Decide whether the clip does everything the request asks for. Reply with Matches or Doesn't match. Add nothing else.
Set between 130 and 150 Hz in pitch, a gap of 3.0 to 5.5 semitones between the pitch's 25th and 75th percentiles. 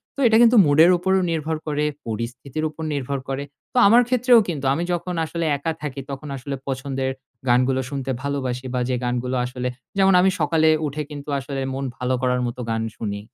Matches